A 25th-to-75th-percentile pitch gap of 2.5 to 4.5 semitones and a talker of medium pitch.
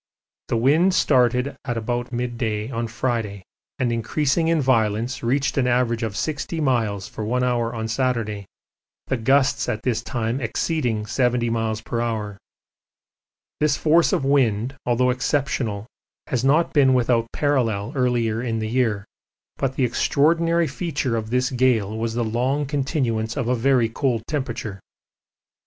No: average, 3.1 semitones; low, 120 Hz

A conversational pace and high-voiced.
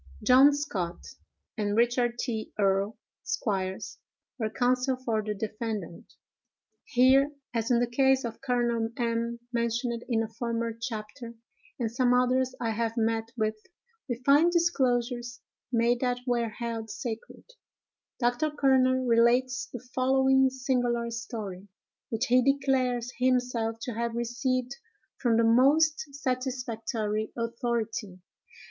No: slow, 125 wpm; high, 240 Hz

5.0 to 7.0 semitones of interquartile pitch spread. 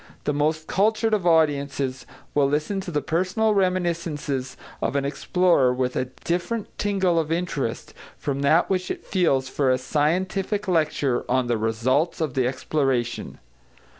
Yes: wide, 5.5 semitones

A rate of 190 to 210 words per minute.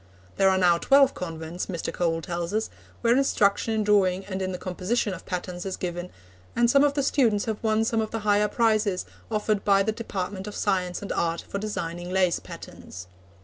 Yes: average, 200 wpm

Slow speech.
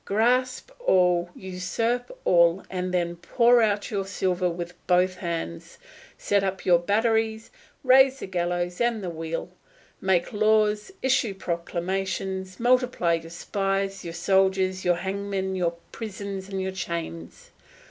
Yes: slow, 130 wpm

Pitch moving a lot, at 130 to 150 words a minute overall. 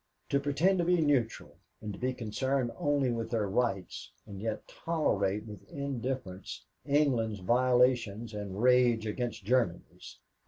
No: average, 4.1 semitones; average, 140 wpm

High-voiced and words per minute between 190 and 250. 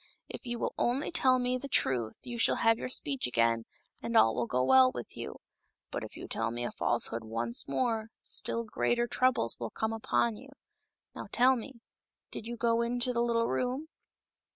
Yes: high, 230 Hz; average, 195 wpm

